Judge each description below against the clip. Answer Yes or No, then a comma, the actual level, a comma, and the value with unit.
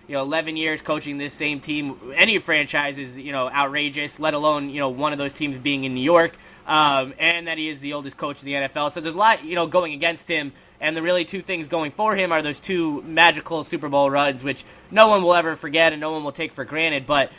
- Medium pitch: Yes, medium, 155 Hz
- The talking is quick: Yes, fast, 260 wpm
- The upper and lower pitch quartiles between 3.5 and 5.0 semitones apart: No, average, 2.7 semitones